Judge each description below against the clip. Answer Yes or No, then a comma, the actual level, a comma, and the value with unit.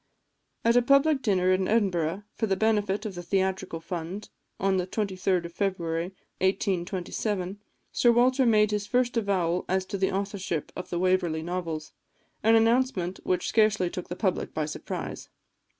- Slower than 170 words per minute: Yes, average, 160 wpm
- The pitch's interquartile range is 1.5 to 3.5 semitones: Yes, average, 3.2 semitones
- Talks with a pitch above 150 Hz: Yes, high, 190 Hz